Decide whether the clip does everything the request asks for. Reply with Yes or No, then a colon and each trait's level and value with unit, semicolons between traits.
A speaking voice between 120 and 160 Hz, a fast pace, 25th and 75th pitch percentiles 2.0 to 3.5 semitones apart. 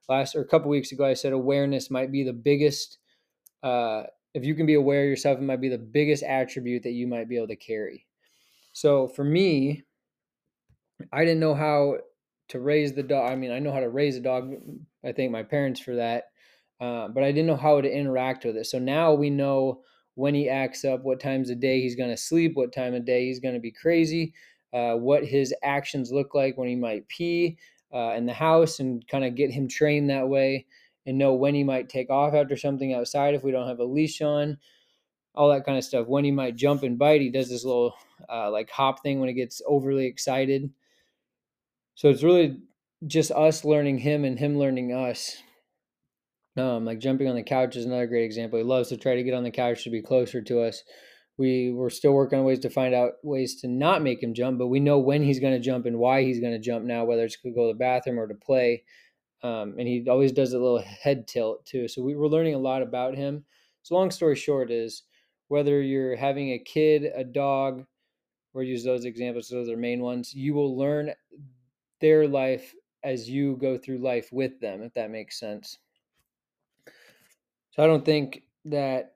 Yes: low, 135 Hz; fast, 220 wpm; narrow, 2.4 semitones